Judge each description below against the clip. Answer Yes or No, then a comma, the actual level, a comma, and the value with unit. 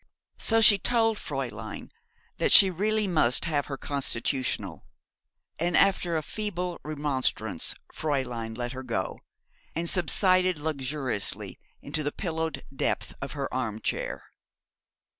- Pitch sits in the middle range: Yes, medium, 150 Hz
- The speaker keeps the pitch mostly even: No, wide, 5.6 semitones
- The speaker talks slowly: Yes, slow, 120 wpm